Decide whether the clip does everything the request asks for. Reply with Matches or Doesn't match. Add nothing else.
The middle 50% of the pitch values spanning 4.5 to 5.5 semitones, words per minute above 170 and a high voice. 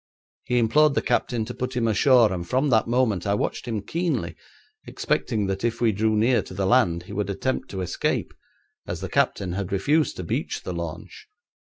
Doesn't match